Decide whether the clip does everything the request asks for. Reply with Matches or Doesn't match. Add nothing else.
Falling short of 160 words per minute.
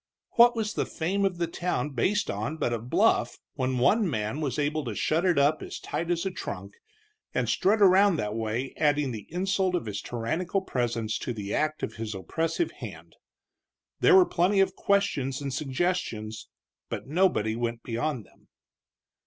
Doesn't match